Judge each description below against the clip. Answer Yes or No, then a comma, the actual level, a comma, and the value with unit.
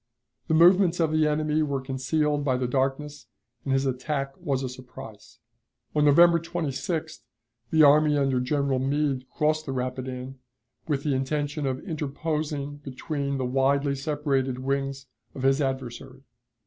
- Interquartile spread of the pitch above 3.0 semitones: No, narrow, 2.4 semitones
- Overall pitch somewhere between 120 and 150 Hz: Yes, medium, 140 Hz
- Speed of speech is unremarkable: Yes, average, 145 wpm